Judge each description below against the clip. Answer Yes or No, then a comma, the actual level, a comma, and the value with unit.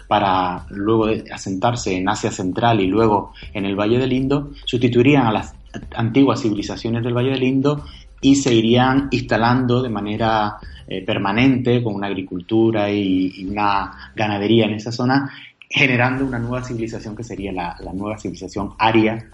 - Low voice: Yes, low, 110 Hz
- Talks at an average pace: Yes, average, 160 wpm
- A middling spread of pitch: Yes, average, 3.8 semitones